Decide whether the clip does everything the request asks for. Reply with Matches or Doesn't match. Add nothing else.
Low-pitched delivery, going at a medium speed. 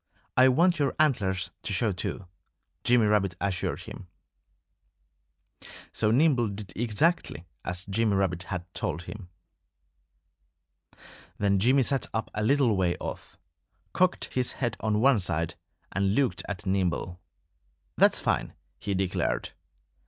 Doesn't match